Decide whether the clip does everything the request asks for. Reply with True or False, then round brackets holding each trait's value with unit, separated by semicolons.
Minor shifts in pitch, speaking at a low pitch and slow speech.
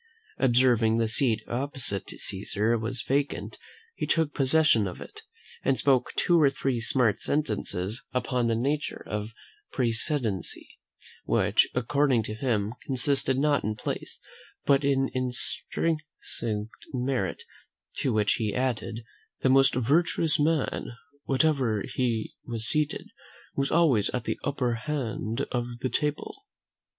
False (3.8 semitones; 125 Hz; 130 wpm)